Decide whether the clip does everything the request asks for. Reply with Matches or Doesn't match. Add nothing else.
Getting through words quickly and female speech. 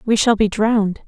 Matches